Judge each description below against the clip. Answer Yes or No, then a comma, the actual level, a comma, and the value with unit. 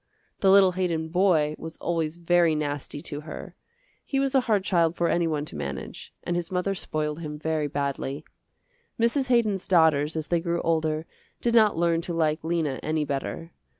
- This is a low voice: No, medium, 165 Hz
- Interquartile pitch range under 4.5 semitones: Yes, average, 2.9 semitones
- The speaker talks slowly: No, average, 185 wpm